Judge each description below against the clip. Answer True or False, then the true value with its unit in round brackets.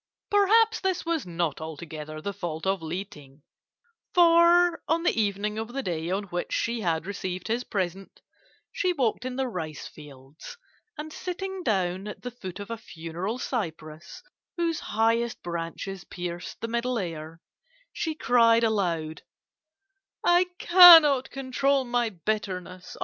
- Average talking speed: True (145 wpm)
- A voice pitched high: True (210 Hz)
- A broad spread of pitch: True (7.6 semitones)